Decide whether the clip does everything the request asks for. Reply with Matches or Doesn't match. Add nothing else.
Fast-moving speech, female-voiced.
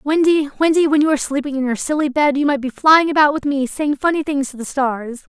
Matches